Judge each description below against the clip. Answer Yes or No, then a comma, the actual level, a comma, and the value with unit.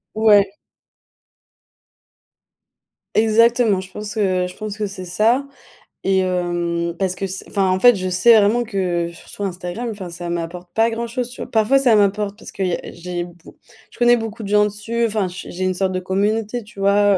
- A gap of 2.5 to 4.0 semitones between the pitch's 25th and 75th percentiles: Yes, average, 3.3 semitones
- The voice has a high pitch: Yes, high, 200 Hz